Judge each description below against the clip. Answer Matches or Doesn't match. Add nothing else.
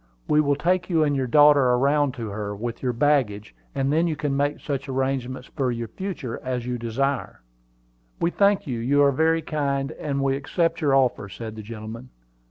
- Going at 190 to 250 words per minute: Matches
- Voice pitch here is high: Doesn't match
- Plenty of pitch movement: Doesn't match